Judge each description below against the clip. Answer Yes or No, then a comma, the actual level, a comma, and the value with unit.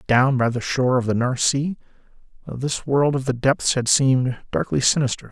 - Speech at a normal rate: Yes, average, 190 wpm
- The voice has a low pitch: Yes, low, 130 Hz